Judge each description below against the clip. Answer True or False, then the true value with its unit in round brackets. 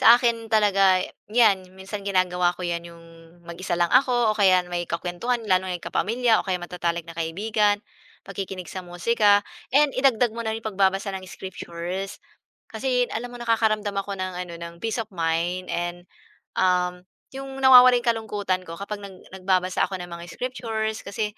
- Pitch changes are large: False (3.8 semitones)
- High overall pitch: True (195 Hz)